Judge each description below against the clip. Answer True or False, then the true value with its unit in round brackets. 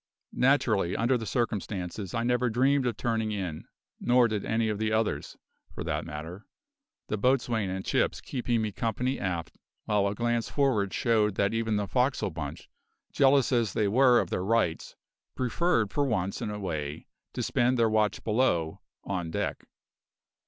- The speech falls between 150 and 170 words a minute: True (165 wpm)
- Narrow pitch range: False (3.7 semitones)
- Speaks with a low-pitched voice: True (110 Hz)